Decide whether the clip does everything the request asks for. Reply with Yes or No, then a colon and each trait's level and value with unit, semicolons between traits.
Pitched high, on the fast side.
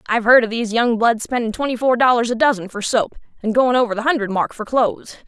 Yes: high, 230 Hz; fast, 250 wpm